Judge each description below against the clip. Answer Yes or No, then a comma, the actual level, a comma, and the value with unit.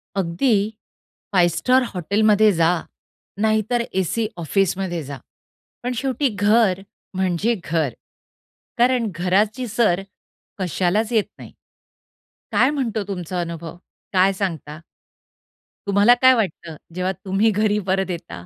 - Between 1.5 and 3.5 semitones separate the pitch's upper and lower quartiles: No, average, 4.1 semitones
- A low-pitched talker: No, high, 195 Hz